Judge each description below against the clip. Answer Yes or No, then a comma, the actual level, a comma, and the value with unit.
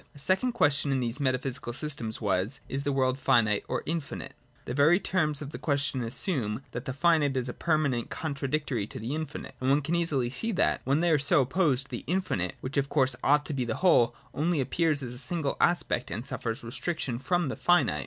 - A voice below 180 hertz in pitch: Yes, medium, 140 Hz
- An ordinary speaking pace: No, fast, 215 wpm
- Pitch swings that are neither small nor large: Yes, average, 3.9 semitones